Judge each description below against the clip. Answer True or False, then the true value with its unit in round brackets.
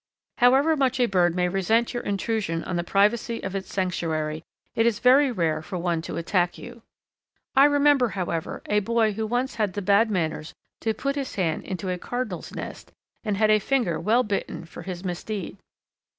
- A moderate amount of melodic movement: True (5.0 semitones)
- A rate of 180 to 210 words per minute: True (190 wpm)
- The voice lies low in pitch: False (205 Hz)